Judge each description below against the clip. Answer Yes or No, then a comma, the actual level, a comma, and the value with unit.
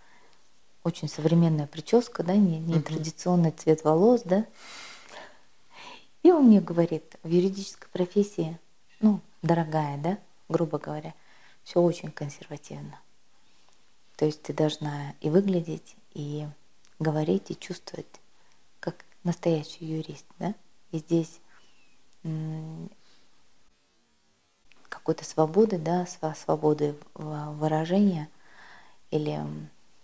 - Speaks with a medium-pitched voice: Yes, medium, 165 Hz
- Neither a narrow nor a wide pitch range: Yes, average, 3.2 semitones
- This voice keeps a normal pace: No, slow, 90 wpm